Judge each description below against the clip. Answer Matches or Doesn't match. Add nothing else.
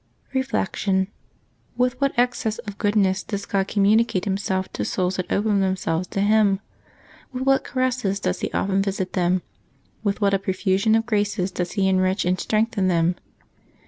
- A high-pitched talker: Matches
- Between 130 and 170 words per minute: Matches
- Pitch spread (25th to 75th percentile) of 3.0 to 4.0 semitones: Doesn't match